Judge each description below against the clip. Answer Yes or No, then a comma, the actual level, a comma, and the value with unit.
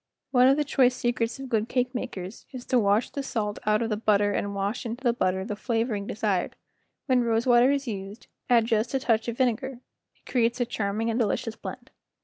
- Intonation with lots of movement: No, average, 2.9 semitones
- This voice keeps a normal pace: No, fast, 215 wpm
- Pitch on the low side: No, high, 230 Hz